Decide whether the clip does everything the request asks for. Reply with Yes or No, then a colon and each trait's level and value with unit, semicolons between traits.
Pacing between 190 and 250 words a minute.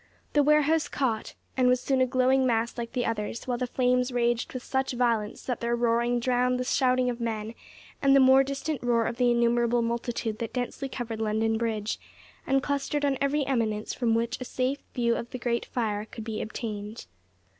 Yes: average, 200 wpm